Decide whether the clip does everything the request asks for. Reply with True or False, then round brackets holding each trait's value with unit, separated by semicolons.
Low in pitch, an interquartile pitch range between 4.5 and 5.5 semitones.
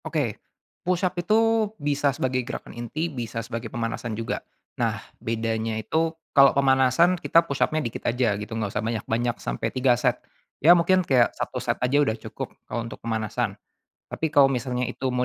True (125 Hz; 4.8 semitones)